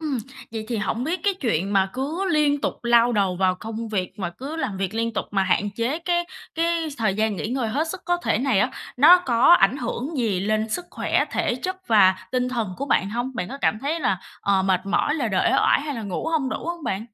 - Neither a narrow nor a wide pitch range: No, wide, 6.6 semitones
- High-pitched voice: Yes, high, 235 Hz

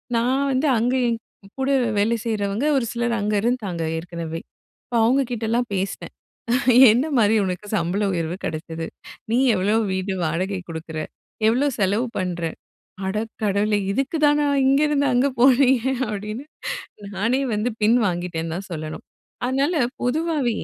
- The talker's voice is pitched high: Yes, high, 215 Hz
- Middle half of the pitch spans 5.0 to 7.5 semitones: Yes, wide, 5.4 semitones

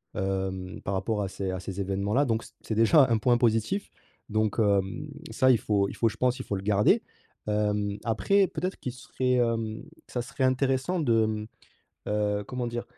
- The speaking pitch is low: Yes, low, 110 Hz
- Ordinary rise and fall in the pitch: Yes, average, 3.8 semitones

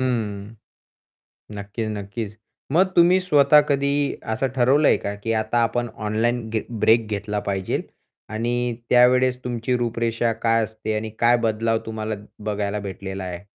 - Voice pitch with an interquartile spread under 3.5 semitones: Yes, average, 2.7 semitones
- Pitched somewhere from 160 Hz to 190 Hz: No, low, 115 Hz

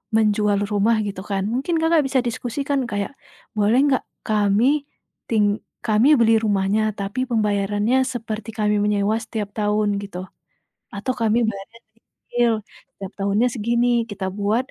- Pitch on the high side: Yes, high, 215 Hz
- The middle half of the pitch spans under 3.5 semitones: Yes, narrow, 2.5 semitones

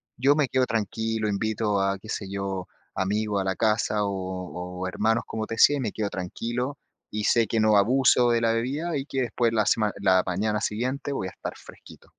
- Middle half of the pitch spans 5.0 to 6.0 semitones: No, average, 3.2 semitones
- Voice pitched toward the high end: No, low, 110 Hz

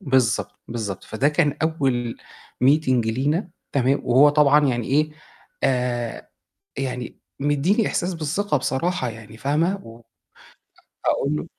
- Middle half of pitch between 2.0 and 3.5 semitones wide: No, average, 4.0 semitones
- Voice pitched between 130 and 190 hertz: Yes, low, 135 Hz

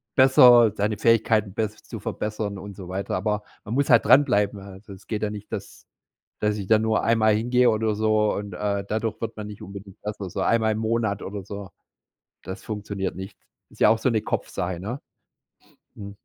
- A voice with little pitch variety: Yes, narrow, 1.8 semitones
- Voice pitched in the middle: No, low, 105 Hz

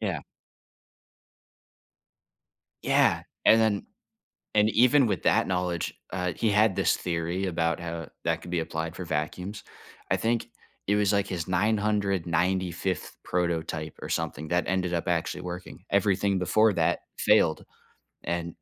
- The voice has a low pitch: Yes, very low, 90 Hz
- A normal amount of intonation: Yes, average, 3.1 semitones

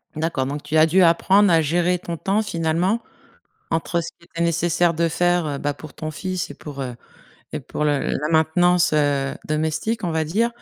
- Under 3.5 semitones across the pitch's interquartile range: Yes, narrow, 2.6 semitones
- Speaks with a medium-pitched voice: Yes, medium, 165 Hz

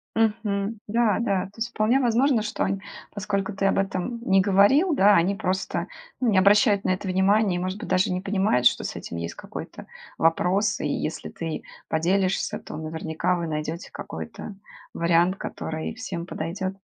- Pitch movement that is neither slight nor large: Yes, average, 3.1 semitones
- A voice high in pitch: Yes, high, 195 Hz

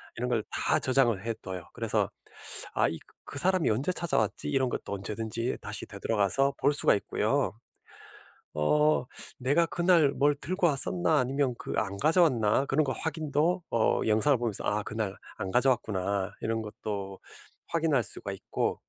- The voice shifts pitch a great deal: Yes, wide, 6.0 semitones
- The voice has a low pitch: Yes, low, 125 Hz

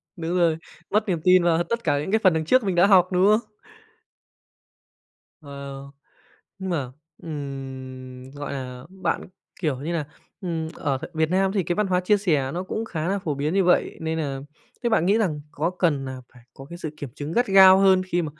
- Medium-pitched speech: Yes, medium, 170 Hz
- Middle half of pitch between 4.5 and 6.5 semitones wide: Yes, average, 4.8 semitones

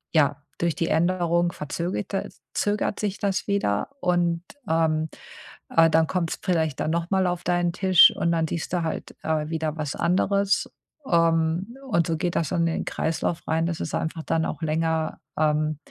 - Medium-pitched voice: Yes, medium, 165 Hz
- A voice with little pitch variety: Yes, narrow, 1.8 semitones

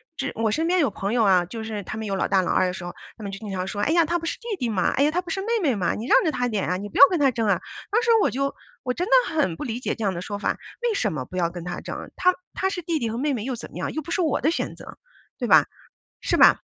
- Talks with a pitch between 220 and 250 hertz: Yes, high, 235 Hz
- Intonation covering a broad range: Yes, wide, 8.4 semitones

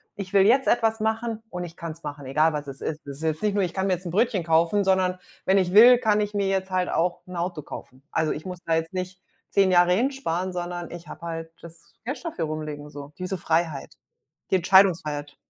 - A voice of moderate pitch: Yes, medium, 180 Hz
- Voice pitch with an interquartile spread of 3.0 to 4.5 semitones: Yes, average, 3.3 semitones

